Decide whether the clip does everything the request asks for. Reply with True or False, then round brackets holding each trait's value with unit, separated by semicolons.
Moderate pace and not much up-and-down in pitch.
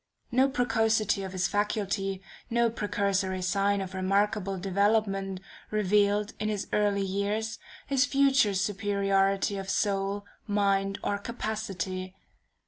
False (115 wpm; 1.7 semitones)